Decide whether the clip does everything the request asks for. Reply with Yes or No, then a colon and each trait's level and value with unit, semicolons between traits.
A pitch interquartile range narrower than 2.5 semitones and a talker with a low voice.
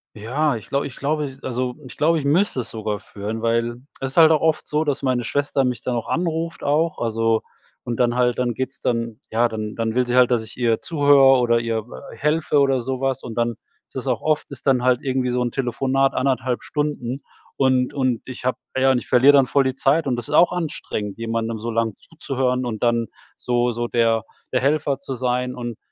No: average, 2.8 semitones; low, 125 Hz